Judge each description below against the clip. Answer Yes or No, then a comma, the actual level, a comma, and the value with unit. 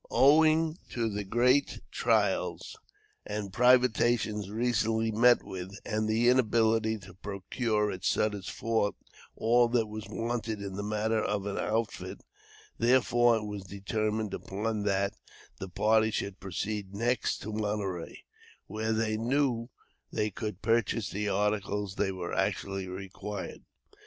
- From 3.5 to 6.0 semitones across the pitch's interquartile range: No, narrow, 2.4 semitones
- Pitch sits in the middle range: No, low, 110 Hz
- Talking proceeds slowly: Yes, slow, 130 wpm